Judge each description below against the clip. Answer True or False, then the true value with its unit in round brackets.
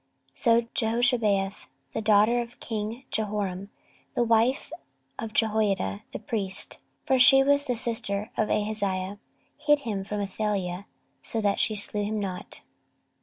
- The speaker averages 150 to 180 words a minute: False (135 wpm)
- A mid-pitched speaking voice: False (215 Hz)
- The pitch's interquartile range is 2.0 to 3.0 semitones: True (2.7 semitones)